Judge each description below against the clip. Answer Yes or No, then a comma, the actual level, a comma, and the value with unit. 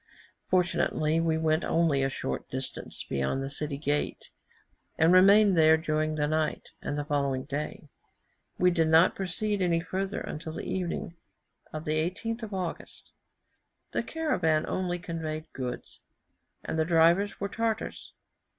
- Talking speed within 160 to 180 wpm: No, average, 145 wpm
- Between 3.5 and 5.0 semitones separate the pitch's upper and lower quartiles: No, average, 3.1 semitones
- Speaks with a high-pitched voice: No, medium, 160 Hz